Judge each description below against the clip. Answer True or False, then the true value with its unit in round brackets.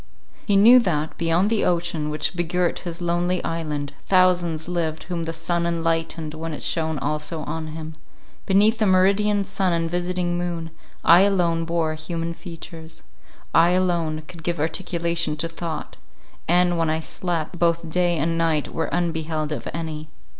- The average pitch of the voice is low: False (170 Hz)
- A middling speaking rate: True (160 wpm)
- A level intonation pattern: True (1.7 semitones)